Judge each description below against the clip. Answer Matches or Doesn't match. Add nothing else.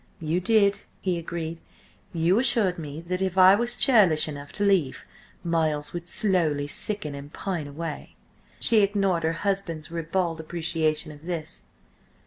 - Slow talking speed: Doesn't match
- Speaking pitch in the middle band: Matches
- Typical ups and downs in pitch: Matches